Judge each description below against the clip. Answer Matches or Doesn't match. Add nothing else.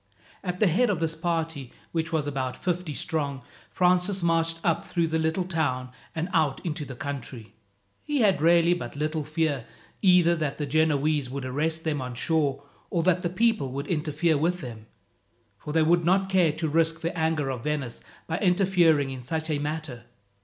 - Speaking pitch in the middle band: Matches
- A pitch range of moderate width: Matches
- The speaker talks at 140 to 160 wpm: Doesn't match